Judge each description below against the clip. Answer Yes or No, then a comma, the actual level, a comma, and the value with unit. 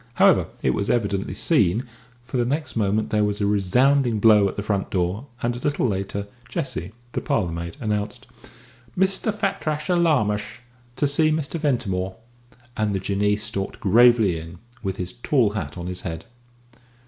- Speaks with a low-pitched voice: Yes, low, 105 Hz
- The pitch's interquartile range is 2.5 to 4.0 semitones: No, average, 4.8 semitones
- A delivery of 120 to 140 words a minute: No, average, 165 wpm